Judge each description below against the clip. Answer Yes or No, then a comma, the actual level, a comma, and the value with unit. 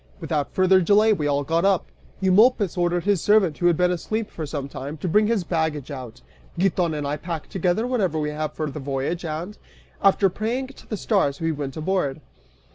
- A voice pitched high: No, medium, 175 Hz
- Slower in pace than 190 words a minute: No, average, 200 wpm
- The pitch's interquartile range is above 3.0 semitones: Yes, average, 4.6 semitones